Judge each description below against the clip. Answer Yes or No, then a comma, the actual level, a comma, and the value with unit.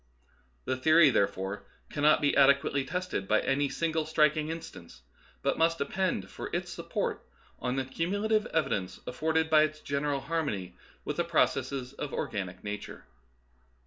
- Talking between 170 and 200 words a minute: No, average, 145 wpm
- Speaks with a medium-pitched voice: Yes, medium, 145 Hz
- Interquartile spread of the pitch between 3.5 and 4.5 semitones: Yes, average, 4.1 semitones